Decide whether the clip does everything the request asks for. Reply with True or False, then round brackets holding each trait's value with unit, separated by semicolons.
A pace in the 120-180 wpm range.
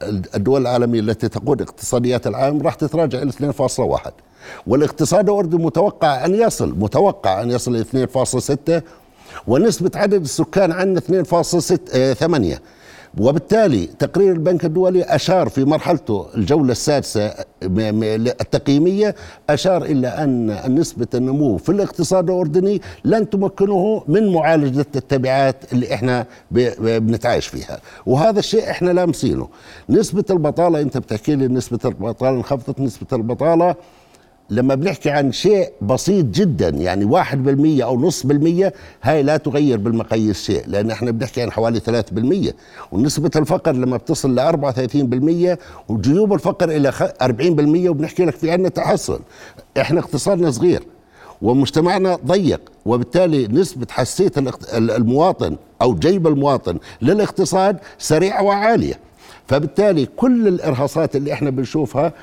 True (125 wpm)